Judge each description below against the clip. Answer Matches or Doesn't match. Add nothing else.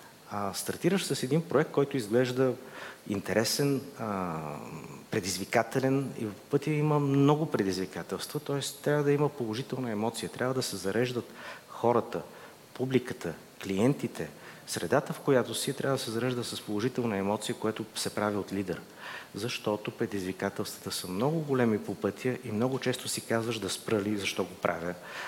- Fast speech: Doesn't match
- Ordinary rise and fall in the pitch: Matches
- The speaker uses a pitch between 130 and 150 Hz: Doesn't match